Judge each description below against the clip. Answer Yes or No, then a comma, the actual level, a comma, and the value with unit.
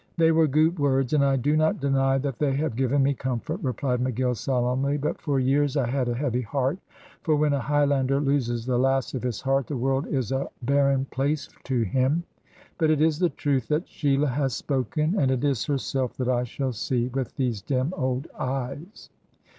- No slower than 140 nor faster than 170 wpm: No, average, 200 wpm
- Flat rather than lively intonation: Yes, narrow, 2.2 semitones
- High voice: No, low, 135 Hz